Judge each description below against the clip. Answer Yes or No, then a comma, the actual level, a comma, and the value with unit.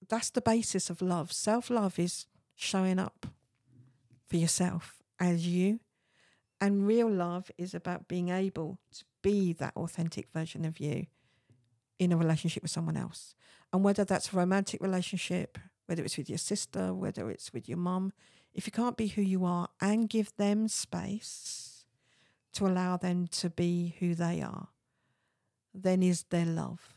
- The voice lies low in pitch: No, medium, 180 Hz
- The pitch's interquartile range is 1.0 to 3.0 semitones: Yes, narrow, 2.6 semitones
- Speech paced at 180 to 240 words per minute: No, average, 160 wpm